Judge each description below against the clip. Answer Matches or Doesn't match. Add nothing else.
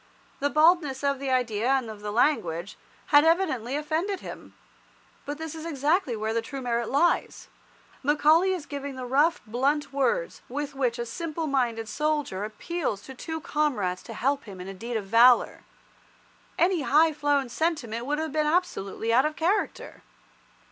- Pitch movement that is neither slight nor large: Matches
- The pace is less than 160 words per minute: Doesn't match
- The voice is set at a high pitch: Matches